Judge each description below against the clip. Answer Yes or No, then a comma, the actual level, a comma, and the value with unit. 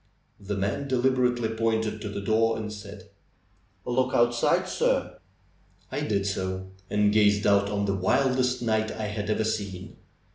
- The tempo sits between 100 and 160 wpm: Yes, average, 150 wpm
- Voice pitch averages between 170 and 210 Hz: No, low, 110 Hz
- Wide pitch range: No, average, 2.8 semitones